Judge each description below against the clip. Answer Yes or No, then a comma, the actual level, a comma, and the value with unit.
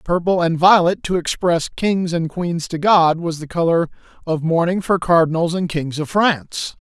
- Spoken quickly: No, average, 185 wpm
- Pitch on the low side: No, medium, 170 Hz